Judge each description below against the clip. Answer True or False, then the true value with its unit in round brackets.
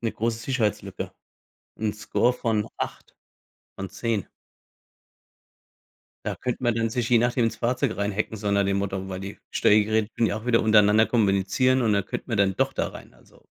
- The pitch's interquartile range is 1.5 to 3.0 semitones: True (2.6 semitones)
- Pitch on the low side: True (110 Hz)